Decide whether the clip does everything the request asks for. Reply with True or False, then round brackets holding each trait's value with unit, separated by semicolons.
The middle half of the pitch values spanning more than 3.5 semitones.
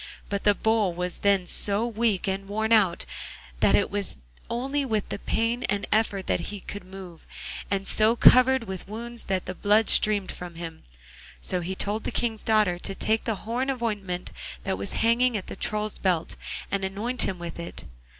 False (3.0 semitones)